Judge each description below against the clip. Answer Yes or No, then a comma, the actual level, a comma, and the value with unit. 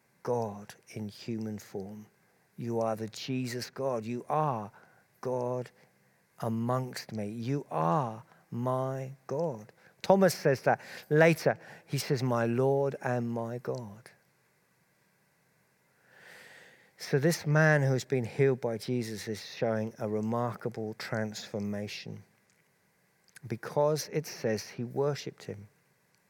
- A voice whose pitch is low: Yes, low, 125 Hz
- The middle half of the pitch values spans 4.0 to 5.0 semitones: Yes, average, 4.4 semitones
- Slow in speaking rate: Yes, slow, 110 wpm